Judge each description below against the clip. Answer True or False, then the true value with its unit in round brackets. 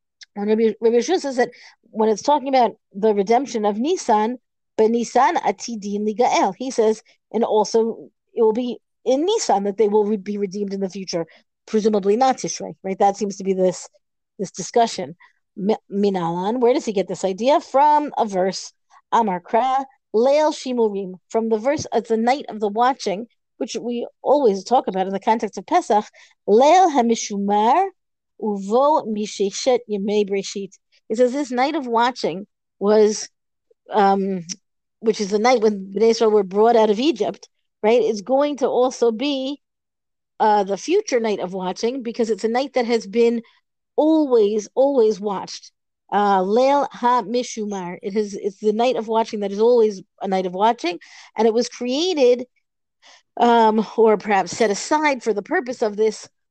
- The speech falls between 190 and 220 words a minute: False (160 wpm)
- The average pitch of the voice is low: False (225 Hz)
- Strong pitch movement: False (3.5 semitones)